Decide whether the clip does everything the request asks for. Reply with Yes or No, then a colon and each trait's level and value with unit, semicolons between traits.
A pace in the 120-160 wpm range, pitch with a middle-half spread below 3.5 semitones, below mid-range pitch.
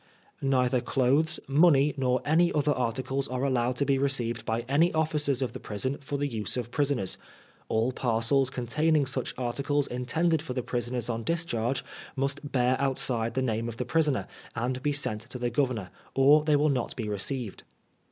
No: average, 180 wpm; average, 3.0 semitones; low, 130 Hz